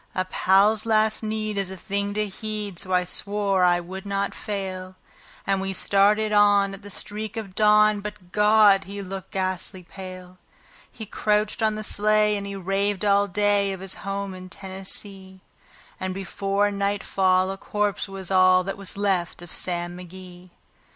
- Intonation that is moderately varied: No, narrow, 1.8 semitones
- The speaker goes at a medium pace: Yes, average, 170 wpm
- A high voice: Yes, high, 195 Hz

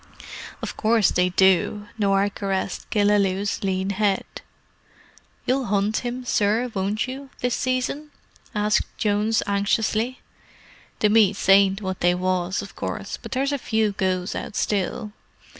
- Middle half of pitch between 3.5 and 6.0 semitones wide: No, narrow, 2.6 semitones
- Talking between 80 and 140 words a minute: Yes, slow, 135 wpm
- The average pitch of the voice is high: Yes, high, 205 Hz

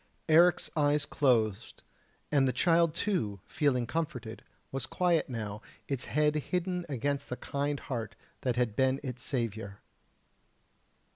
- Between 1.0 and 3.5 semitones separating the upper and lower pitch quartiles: No, average, 4.6 semitones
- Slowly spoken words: Yes, slow, 130 wpm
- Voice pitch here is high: No, medium, 140 Hz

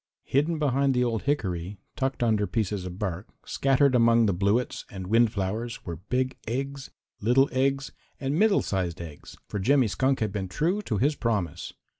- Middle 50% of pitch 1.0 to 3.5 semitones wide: No, wide, 5.5 semitones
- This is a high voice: No, low, 115 Hz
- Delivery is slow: No, average, 175 wpm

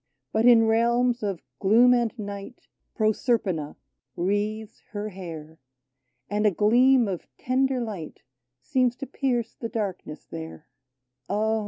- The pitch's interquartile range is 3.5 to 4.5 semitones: Yes, average, 3.8 semitones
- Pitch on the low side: No, high, 215 Hz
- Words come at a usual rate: No, slow, 130 wpm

